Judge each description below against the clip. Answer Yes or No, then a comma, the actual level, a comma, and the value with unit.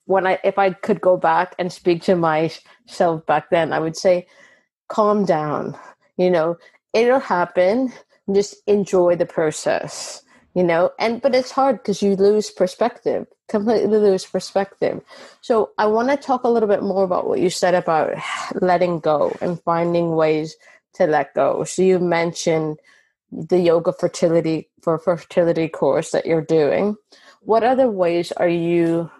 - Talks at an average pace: Yes, average, 160 wpm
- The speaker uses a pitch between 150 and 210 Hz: Yes, medium, 185 Hz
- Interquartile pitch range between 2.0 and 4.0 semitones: Yes, average, 3.5 semitones